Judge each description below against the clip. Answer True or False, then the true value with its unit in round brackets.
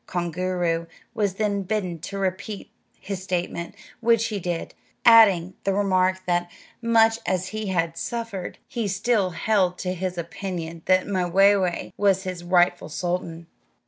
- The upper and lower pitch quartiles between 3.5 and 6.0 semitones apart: False (2.5 semitones)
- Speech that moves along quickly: False (140 wpm)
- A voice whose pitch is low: False (185 Hz)